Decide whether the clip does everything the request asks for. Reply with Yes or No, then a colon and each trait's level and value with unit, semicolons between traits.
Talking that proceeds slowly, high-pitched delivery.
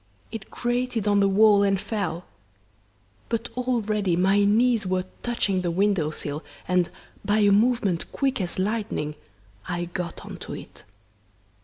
No: average, 145 wpm; high, 200 Hz